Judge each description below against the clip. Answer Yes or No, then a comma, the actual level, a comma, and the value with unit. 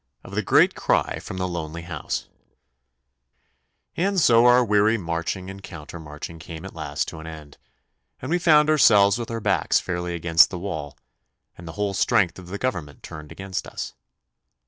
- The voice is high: No, very low, 90 Hz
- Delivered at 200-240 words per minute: No, average, 175 wpm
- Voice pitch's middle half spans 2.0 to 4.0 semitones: No, average, 4.5 semitones